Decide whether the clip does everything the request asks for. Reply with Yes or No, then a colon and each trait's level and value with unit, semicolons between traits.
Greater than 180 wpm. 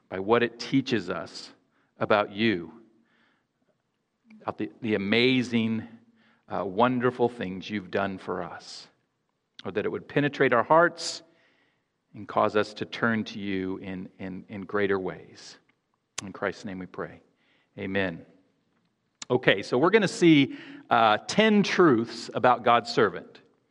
No: average, 140 wpm